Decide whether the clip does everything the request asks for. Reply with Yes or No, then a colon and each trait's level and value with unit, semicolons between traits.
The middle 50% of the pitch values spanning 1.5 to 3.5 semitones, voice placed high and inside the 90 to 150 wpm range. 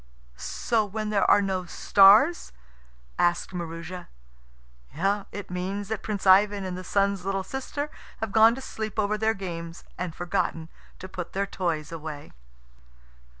Yes: average, 3.0 semitones; high, 195 Hz; average, 145 wpm